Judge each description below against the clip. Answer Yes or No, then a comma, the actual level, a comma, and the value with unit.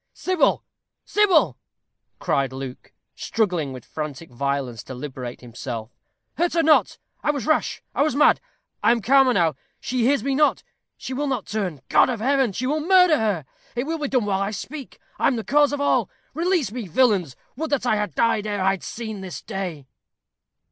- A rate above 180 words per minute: Yes, average, 190 wpm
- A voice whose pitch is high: Yes, high, 225 Hz